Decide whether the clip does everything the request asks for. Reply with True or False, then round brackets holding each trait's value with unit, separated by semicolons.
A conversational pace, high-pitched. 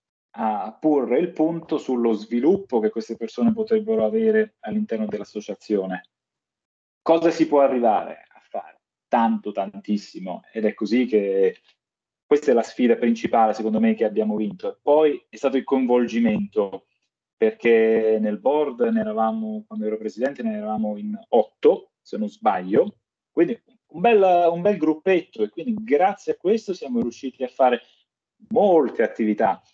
False (145 wpm; 130 Hz)